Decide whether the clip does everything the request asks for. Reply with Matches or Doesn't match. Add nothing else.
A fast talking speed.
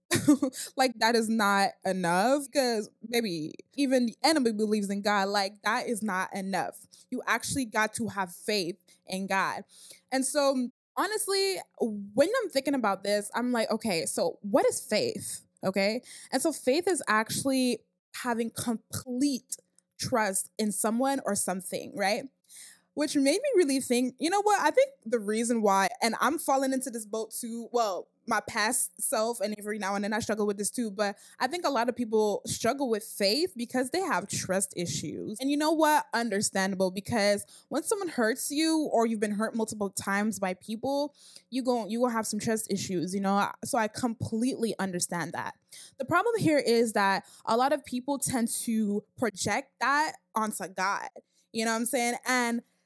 Doesn't match